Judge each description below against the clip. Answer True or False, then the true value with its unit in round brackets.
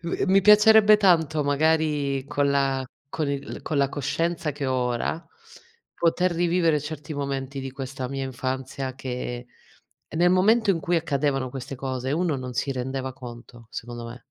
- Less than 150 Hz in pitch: True (140 Hz)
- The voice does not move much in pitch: False (4.0 semitones)